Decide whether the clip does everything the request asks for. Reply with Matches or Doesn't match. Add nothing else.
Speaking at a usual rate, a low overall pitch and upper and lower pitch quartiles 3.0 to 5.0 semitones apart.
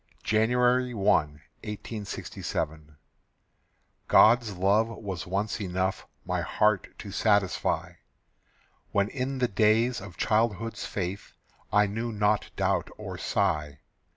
Doesn't match